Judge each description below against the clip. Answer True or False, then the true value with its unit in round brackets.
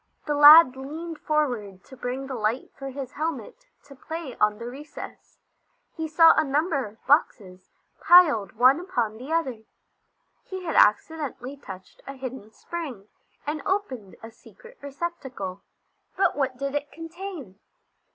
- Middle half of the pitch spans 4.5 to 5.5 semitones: True (5.2 semitones)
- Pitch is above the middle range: True (275 Hz)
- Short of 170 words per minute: True (145 wpm)